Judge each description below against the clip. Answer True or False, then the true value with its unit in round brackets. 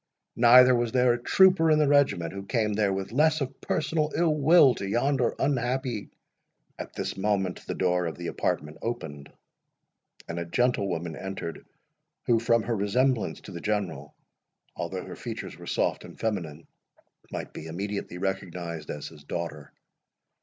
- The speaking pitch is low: True (105 Hz)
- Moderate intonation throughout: False (6.6 semitones)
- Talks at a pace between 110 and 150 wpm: False (160 wpm)